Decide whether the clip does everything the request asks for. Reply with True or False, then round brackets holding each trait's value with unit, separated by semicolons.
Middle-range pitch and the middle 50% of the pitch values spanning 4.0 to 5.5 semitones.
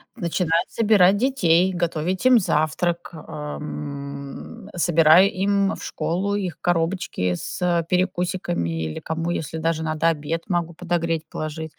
False (170 Hz; 2.6 semitones)